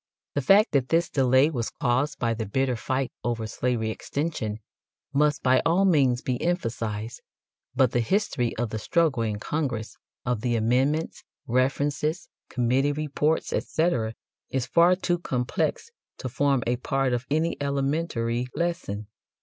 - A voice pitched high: No, low, 130 Hz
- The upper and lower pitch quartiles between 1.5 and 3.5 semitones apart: No, average, 4.1 semitones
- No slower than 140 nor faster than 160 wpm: Yes, average, 145 wpm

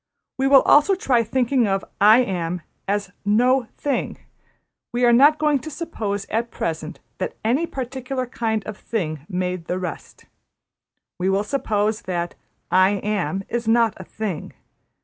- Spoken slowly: No, average, 150 wpm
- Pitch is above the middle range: Yes, high, 220 Hz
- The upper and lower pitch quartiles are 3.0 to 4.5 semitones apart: No, average, 5.1 semitones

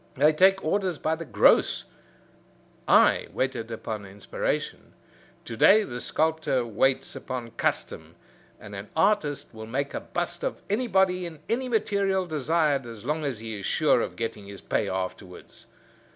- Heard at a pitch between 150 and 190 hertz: No, medium, 140 Hz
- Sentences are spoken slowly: No, average, 150 wpm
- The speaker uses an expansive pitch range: Yes, wide, 8.2 semitones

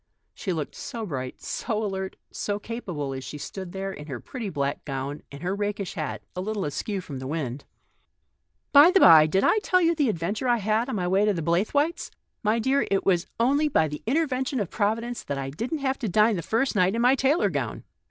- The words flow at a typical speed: No, fast, 225 wpm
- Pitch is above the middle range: Yes, high, 205 Hz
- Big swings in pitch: Yes, wide, 6.9 semitones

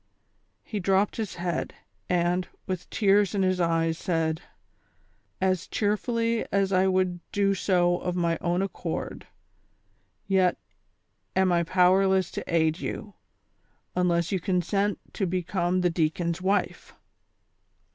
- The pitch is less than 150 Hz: No, medium, 185 Hz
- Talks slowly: Yes, slow, 125 wpm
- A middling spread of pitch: No, narrow, 2.0 semitones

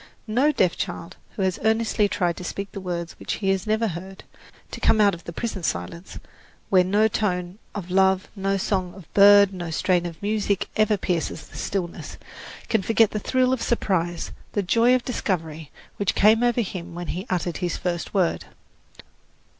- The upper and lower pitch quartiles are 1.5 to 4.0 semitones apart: Yes, average, 3.4 semitones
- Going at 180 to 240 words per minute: Yes, average, 185 wpm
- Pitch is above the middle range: Yes, high, 195 Hz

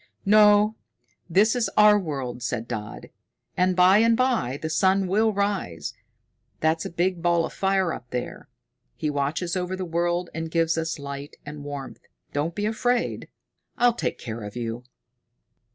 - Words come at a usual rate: Yes, average, 160 wpm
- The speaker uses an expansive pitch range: Yes, wide, 5.9 semitones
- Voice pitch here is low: No, medium, 170 Hz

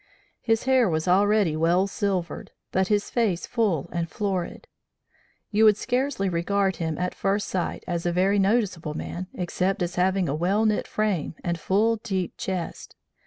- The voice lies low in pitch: No, high, 190 Hz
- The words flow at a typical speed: Yes, average, 165 wpm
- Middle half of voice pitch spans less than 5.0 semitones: Yes, average, 3.2 semitones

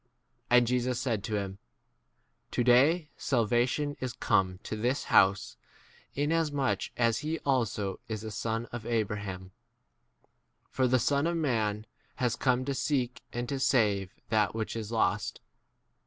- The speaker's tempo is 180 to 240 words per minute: No, average, 150 wpm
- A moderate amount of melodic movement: Yes, average, 3.6 semitones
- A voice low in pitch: Yes, low, 120 Hz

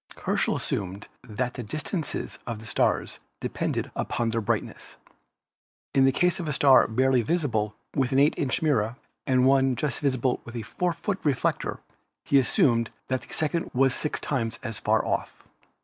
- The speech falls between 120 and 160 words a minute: No, average, 170 wpm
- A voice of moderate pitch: No, low, 130 Hz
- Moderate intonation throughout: Yes, average, 3.8 semitones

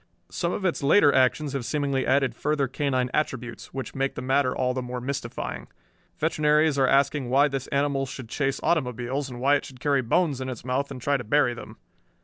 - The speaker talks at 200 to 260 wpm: Yes, fast, 205 wpm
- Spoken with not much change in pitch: Yes, narrow, 2.1 semitones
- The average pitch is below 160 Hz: Yes, low, 135 Hz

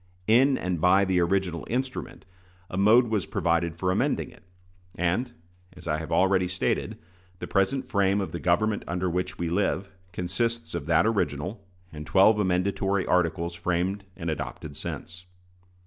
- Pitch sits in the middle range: No, very low, 90 Hz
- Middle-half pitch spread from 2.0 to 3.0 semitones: Yes, average, 2.7 semitones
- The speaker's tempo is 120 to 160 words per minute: Yes, average, 155 wpm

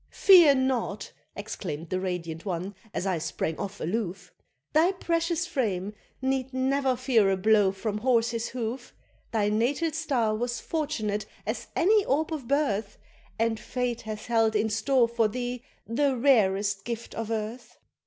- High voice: Yes, high, 230 Hz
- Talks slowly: No, average, 150 wpm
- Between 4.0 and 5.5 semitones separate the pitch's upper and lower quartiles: Yes, average, 4.4 semitones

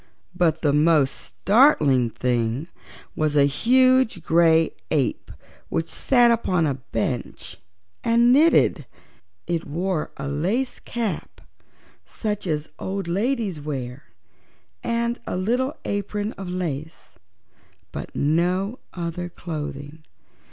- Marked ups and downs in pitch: Yes, wide, 6.9 semitones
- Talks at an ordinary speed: No, slow, 110 wpm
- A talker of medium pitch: Yes, medium, 170 Hz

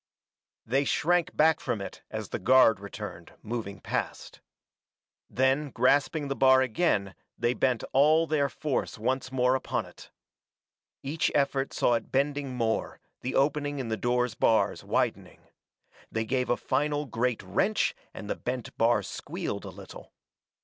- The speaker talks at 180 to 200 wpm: No, average, 150 wpm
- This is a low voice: Yes, low, 130 Hz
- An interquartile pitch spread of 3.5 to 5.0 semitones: Yes, average, 3.8 semitones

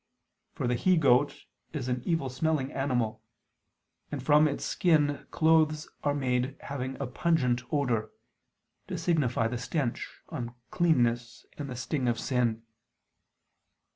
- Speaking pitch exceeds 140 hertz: No, low, 130 Hz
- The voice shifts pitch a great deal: No, average, 3.6 semitones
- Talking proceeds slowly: Yes, slow, 130 wpm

